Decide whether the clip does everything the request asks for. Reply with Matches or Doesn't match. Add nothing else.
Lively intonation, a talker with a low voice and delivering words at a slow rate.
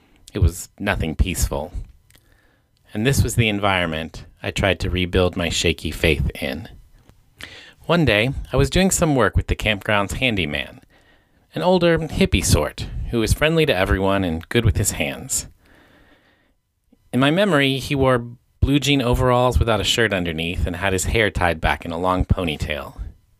Doesn't match